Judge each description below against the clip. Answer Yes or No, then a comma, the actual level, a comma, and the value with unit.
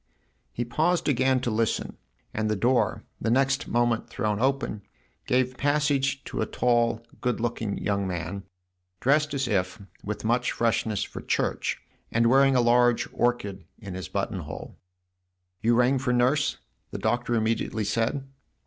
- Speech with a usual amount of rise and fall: Yes, average, 3.6 semitones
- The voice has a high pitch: No, low, 120 Hz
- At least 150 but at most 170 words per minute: Yes, average, 155 wpm